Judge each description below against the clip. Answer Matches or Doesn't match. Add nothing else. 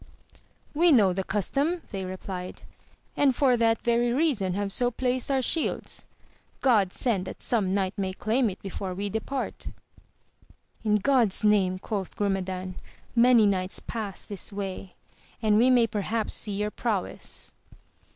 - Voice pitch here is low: Doesn't match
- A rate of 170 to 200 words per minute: Doesn't match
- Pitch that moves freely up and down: Doesn't match